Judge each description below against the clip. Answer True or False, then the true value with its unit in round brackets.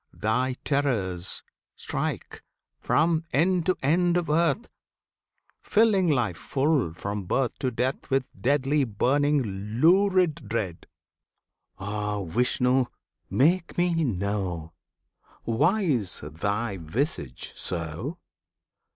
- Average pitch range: False (7.9 semitones)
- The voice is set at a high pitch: False (130 Hz)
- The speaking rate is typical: False (100 wpm)